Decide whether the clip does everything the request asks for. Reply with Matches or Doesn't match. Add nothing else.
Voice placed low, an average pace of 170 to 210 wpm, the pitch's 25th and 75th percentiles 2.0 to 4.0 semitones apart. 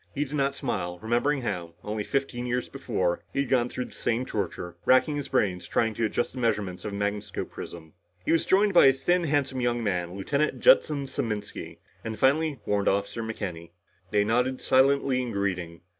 Doesn't match